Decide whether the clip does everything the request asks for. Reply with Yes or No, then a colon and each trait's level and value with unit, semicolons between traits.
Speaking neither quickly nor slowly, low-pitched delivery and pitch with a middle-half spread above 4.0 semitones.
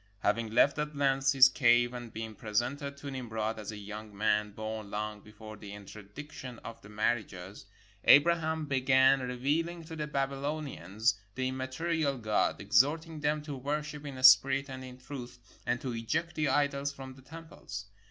Yes: average, 165 wpm; low, 130 Hz; average, 4.6 semitones